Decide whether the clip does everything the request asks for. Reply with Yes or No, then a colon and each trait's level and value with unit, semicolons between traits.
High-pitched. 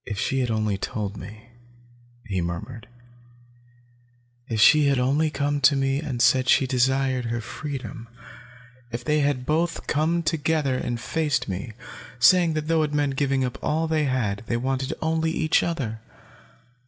No: low, 135 Hz